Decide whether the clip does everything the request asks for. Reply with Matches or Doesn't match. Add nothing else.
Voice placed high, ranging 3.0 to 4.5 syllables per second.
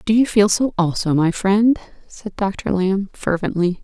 Matches